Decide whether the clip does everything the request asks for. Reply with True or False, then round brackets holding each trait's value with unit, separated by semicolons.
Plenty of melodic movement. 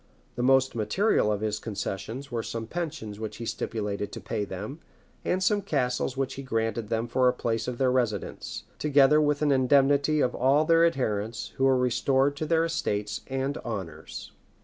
False (4.3 semitones)